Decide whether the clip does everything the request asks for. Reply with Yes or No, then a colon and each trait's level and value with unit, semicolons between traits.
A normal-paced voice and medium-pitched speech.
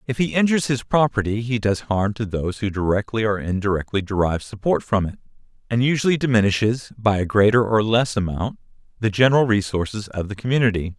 No: average, 180 wpm; low, 110 Hz